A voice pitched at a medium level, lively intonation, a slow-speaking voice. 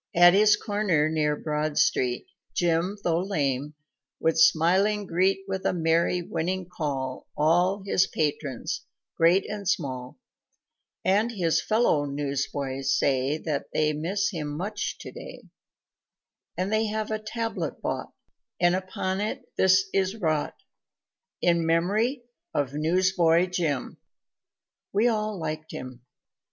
No: medium, 170 Hz; average, 4.5 semitones; slow, 125 wpm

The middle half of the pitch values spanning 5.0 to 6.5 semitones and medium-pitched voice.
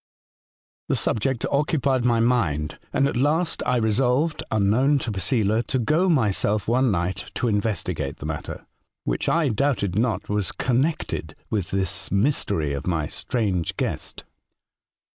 No: wide, 5.4 semitones; low, 115 Hz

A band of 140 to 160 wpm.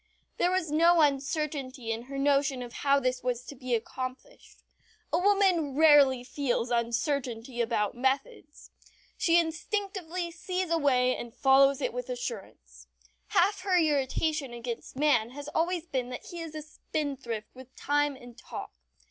Yes: average, 150 wpm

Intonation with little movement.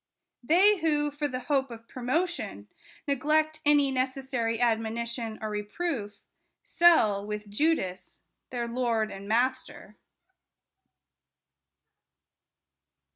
No: average, 5.0 semitones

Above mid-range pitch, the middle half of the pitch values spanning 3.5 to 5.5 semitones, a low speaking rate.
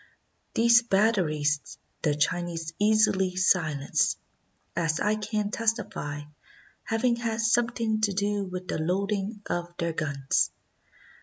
Yes: high, 195 Hz; average, 5.0 semitones; slow, 110 wpm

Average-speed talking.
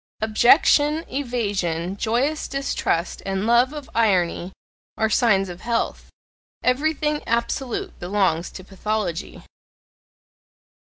No: slow, 95 wpm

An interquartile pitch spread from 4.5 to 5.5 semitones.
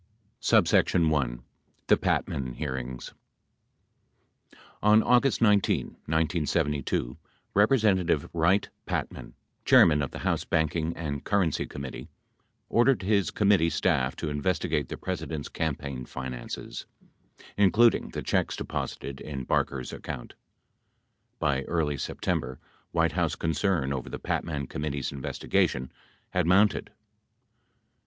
Yes: average, 5.2 semitones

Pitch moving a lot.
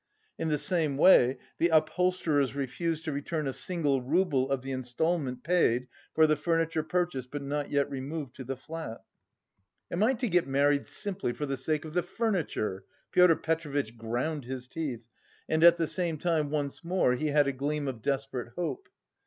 No: average, 3.8 semitones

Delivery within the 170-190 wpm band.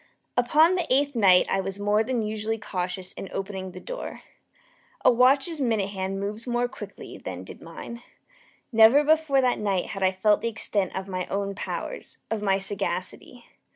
Yes: average, 175 wpm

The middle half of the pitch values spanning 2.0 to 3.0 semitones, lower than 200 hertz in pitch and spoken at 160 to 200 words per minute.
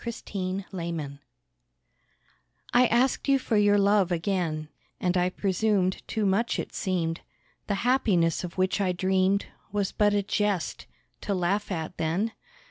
No: narrow, 2.6 semitones; high, 190 Hz; slow, 135 wpm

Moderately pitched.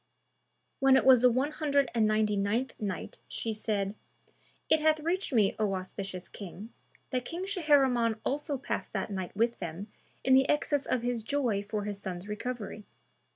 No: high, 230 Hz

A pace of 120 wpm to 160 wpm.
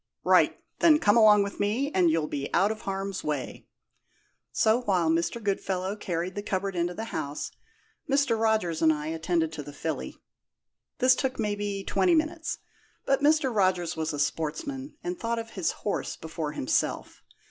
No: average, 170 wpm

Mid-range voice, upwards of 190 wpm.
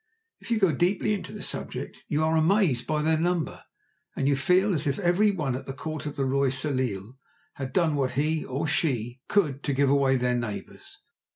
Yes: medium, 145 Hz; fast, 205 wpm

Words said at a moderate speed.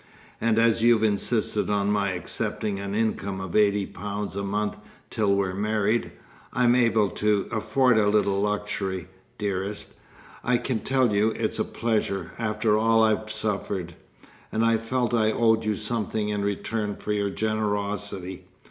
Yes: average, 155 wpm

